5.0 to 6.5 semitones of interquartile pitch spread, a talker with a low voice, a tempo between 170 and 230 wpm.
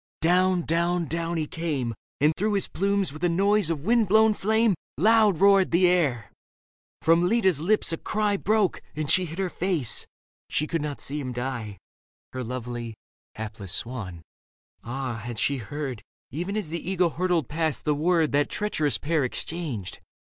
No: wide, 5.6 semitones; medium, 165 Hz; average, 175 wpm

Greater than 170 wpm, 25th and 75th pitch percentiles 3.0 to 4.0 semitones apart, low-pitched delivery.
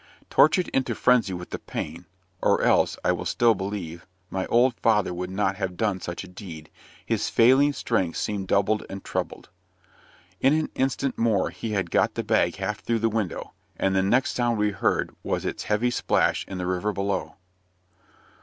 Yes: average, 180 wpm; average, 3.7 semitones; low, 105 Hz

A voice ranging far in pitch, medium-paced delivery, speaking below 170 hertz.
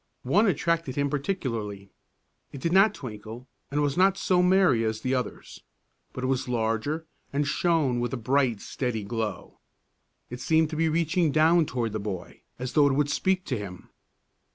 Yes: wide, 5.7 semitones; average, 175 wpm; low, 135 Hz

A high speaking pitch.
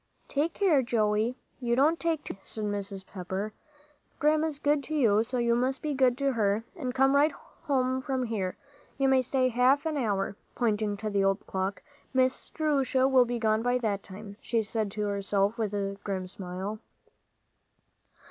Yes: high, 235 Hz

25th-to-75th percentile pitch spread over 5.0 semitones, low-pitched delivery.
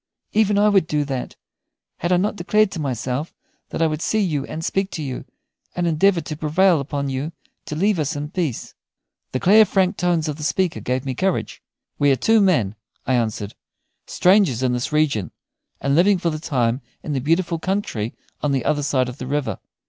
No: wide, 5.4 semitones; medium, 155 Hz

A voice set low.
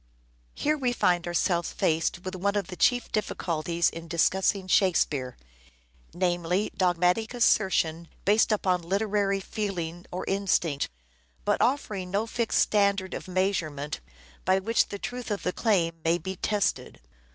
No: medium, 185 Hz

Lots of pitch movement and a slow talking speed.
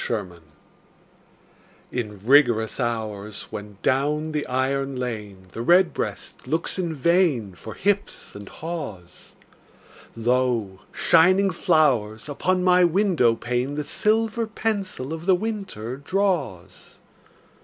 Yes: wide, 8.3 semitones; slow, 110 wpm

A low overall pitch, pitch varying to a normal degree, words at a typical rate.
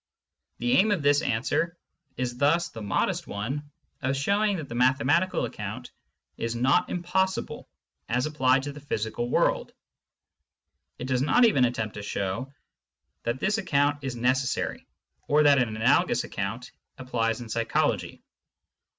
Yes: low, 130 Hz; average, 3.9 semitones; average, 145 wpm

